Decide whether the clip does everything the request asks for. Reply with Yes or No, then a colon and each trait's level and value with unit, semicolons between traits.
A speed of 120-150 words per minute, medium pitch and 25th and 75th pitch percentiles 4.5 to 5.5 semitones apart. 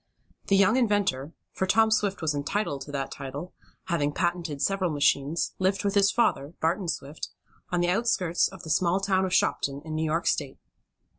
No: average, 180 wpm; medium, 175 Hz; average, 5.0 semitones